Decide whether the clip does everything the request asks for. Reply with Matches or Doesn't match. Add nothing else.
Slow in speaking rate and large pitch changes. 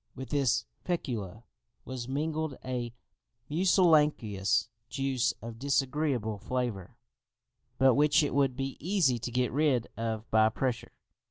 Doesn't match